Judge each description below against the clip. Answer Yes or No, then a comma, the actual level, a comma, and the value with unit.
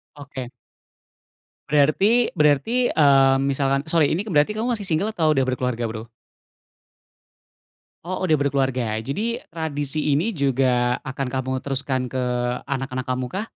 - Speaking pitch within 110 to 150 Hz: Yes, medium, 140 Hz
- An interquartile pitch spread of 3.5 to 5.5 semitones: No, average, 3.1 semitones